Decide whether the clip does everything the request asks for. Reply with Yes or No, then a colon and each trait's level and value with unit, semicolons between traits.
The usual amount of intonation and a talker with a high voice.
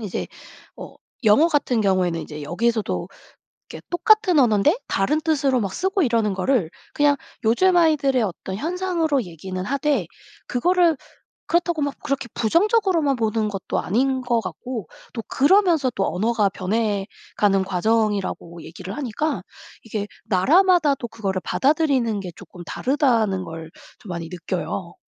No: wide, 7.5 semitones; high, 235 Hz